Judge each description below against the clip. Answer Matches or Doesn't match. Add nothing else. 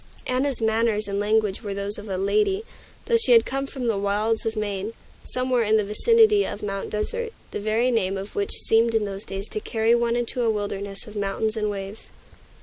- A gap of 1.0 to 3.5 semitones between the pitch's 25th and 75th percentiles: Matches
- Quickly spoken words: Matches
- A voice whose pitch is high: Matches